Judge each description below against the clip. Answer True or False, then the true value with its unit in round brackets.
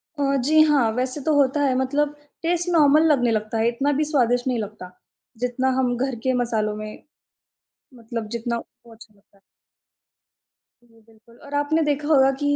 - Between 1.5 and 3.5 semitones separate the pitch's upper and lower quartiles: False (4.1 semitones)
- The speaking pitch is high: True (255 Hz)